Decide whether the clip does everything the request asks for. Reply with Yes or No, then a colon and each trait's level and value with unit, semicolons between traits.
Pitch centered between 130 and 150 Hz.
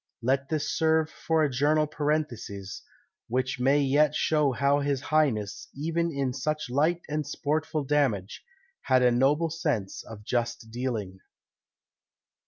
Yes: medium, 140 Hz